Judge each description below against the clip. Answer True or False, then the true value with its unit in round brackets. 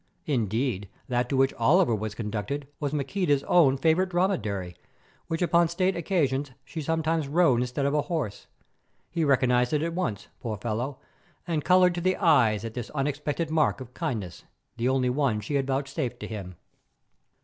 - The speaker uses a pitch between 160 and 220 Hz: False (140 Hz)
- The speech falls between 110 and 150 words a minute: False (170 wpm)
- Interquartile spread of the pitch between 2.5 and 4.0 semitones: False (5.6 semitones)